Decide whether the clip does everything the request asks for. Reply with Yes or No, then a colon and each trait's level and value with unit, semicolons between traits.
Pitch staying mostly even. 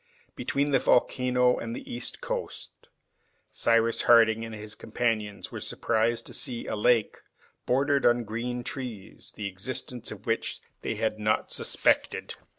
Yes: narrow, 2.2 semitones